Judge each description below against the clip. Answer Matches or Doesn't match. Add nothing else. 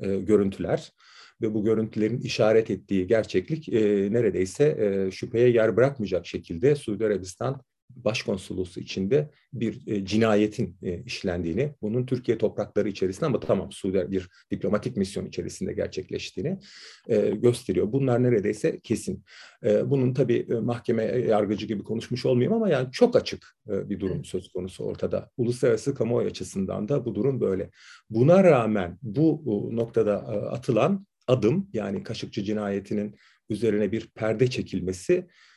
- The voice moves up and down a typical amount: Matches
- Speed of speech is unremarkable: Matches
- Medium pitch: Doesn't match